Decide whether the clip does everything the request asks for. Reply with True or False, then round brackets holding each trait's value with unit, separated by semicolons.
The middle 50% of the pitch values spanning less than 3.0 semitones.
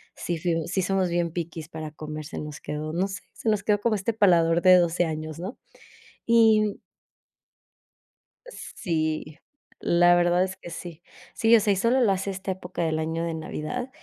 False (3.6 semitones)